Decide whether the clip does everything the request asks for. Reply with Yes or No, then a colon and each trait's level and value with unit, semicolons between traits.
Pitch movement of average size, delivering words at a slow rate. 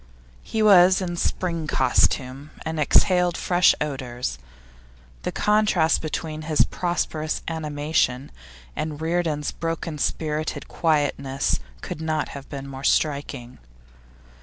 Yes: average, 3.2 semitones; slow, 110 wpm